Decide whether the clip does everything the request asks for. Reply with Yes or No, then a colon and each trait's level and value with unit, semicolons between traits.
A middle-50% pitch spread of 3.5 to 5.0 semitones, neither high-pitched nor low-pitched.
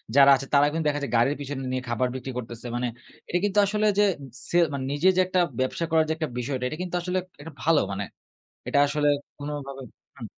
Yes: average, 3.9 semitones; medium, 145 Hz